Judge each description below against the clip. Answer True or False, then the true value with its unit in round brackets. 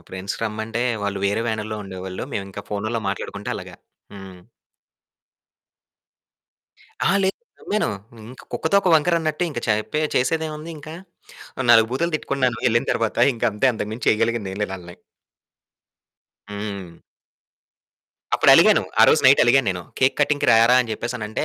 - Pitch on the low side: True (115 Hz)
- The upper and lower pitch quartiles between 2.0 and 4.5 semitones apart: False (5.1 semitones)